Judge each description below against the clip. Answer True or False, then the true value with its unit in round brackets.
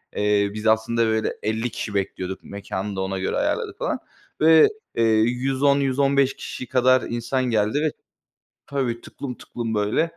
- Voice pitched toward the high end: False (115 Hz)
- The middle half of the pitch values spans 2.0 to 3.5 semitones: False (4.2 semitones)